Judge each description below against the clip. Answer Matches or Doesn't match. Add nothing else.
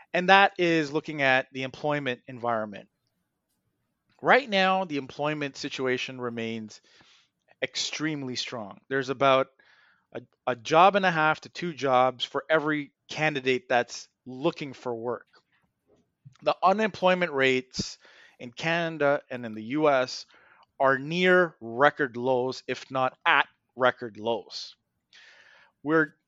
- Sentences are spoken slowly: Matches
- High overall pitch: Doesn't match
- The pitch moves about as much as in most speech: Matches